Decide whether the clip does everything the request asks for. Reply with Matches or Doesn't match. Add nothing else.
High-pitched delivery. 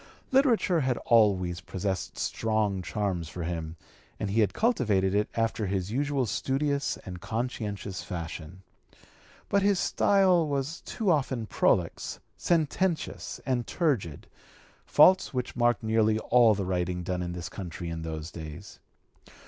Doesn't match